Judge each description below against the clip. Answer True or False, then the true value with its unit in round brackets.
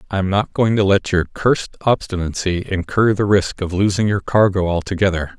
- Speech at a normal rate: True (190 wpm)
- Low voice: True (95 Hz)